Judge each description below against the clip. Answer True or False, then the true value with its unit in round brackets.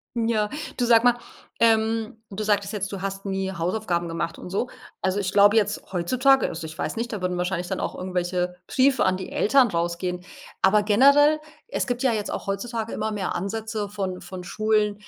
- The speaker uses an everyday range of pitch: True (3.5 semitones)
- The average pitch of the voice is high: True (205 Hz)